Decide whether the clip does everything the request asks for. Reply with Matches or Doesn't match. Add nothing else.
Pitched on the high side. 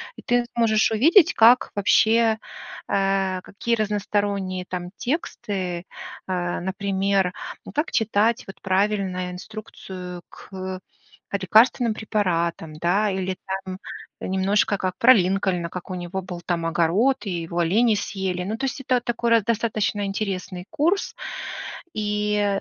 Matches